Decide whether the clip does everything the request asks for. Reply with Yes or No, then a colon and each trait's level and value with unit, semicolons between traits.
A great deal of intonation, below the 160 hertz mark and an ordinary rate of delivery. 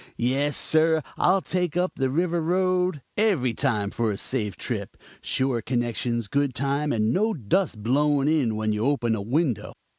Yes: wide, 5.7 semitones; medium, 140 Hz; average, 160 wpm